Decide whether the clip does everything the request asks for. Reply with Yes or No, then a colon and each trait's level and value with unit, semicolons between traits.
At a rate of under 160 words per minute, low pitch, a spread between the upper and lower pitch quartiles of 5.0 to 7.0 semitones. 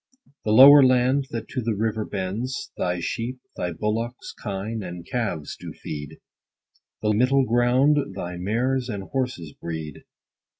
Yes: average, 140 wpm; low, 115 Hz; average, 5.3 semitones